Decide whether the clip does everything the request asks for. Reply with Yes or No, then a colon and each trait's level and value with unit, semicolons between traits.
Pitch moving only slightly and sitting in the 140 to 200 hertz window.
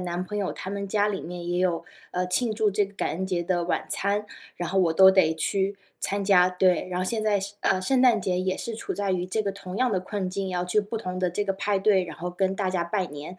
Yes: narrow, 2.1 semitones; high, 190 Hz